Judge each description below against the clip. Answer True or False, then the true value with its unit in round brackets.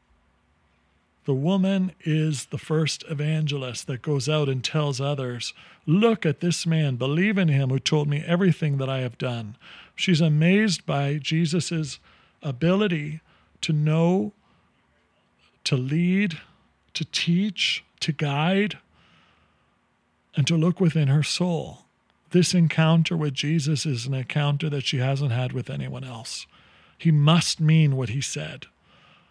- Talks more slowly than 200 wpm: True (135 wpm)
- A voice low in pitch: False (155 Hz)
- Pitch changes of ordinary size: True (3.8 semitones)